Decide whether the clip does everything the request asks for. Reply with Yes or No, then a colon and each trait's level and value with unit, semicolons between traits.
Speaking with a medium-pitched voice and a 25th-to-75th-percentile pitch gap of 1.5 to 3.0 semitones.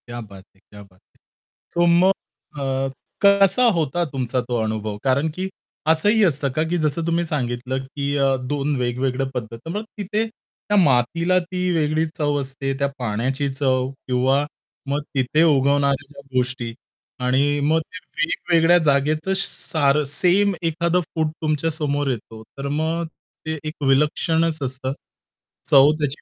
No: medium, 145 Hz; average, 3.8 semitones